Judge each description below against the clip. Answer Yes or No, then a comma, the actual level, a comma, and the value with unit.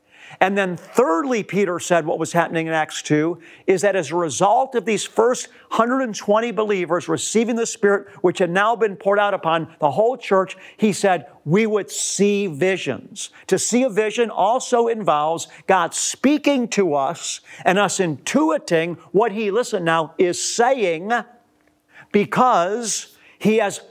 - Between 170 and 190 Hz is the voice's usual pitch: No, high, 200 Hz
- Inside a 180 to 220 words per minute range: No, average, 155 wpm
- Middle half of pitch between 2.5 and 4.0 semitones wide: No, average, 4.9 semitones